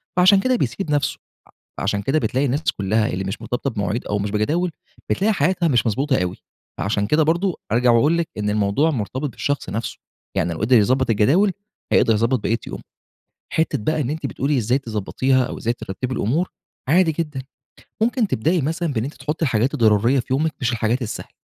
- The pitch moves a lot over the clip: Yes, wide, 6.2 semitones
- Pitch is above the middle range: No, low, 130 Hz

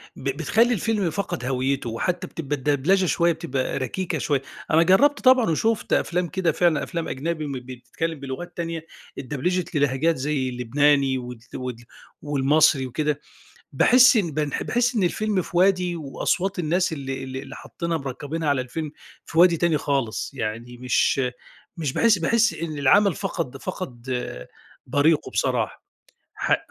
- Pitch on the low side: No, medium, 155 Hz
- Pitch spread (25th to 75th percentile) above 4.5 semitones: Yes, average, 5.0 semitones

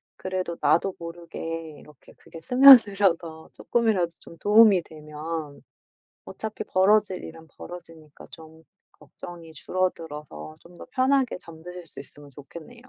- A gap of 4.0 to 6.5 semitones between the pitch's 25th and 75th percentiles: No, average, 3.5 semitones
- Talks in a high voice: No, medium, 170 Hz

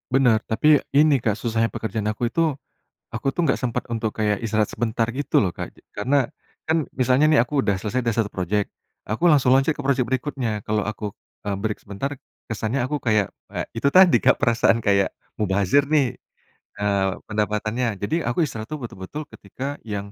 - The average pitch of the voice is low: Yes, low, 115 Hz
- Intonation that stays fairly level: No, average, 4.2 semitones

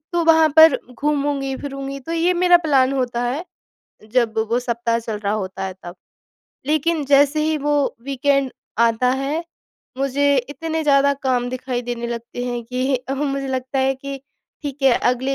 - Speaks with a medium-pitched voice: No, very high, 270 Hz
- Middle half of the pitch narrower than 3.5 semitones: Yes, average, 2.9 semitones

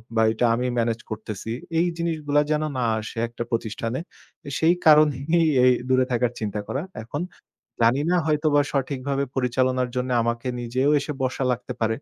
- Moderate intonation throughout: Yes, average, 3.8 semitones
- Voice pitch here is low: Yes, low, 130 Hz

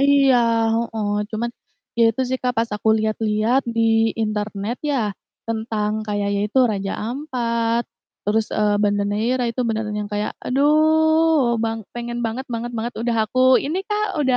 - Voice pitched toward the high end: Yes, high, 230 Hz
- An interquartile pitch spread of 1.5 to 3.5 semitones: Yes, average, 3.2 semitones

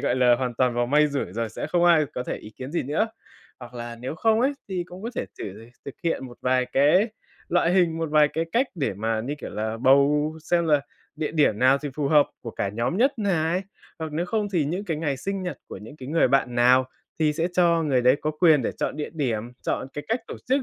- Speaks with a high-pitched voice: No, medium, 150 Hz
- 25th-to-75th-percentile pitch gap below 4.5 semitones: No, average, 5.2 semitones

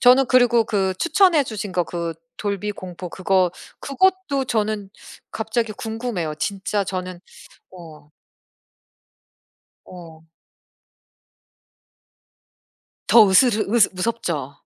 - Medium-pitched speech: No, high, 205 Hz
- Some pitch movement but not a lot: Yes, average, 4.6 semitones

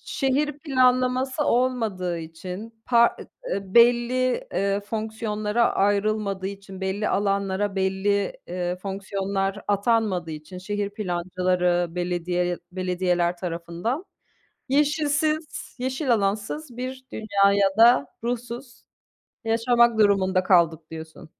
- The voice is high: Yes, high, 200 Hz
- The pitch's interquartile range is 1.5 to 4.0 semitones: No, average, 4.5 semitones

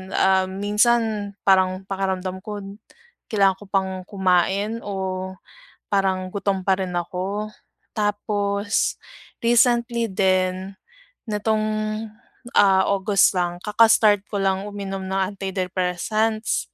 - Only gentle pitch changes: Yes, narrow, 1.7 semitones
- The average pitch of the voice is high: Yes, high, 195 Hz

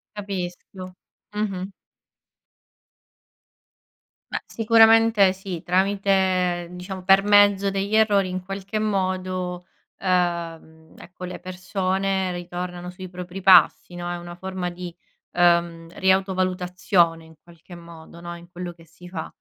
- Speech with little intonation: Yes, narrow, 1.7 semitones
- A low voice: No, medium, 185 Hz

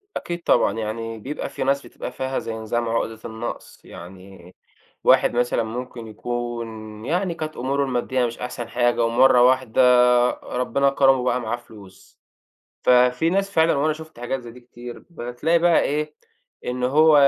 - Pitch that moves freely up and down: No, average, 3.1 semitones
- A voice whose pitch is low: Yes, low, 125 Hz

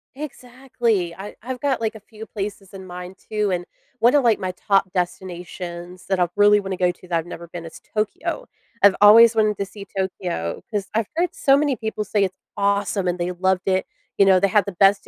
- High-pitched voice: Yes, high, 195 Hz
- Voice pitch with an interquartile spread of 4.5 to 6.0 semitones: No, average, 3.3 semitones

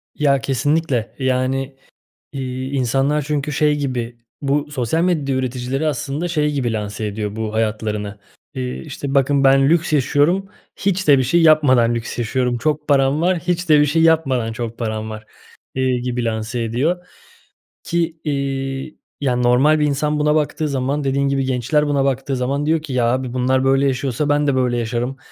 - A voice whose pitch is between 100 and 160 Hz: Yes, low, 135 Hz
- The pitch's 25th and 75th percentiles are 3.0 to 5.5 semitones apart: Yes, average, 3.3 semitones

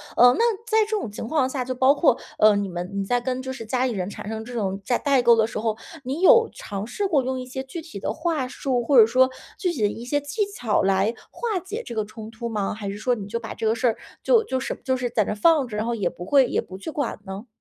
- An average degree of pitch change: Yes, average, 4.2 semitones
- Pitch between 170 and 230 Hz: No, high, 245 Hz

